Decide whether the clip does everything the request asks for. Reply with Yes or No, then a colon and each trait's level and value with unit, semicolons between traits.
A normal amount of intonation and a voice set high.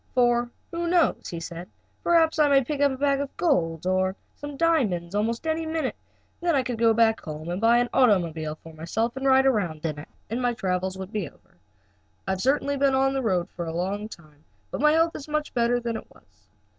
No: wide, 7.5 semitones; high, 235 Hz